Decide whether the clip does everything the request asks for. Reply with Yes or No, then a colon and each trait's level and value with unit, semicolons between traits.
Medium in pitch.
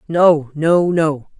Yes: medium, 160 Hz